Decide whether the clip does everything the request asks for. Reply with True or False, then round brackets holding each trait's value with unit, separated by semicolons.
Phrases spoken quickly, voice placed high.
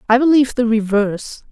False (160 wpm; 235 Hz)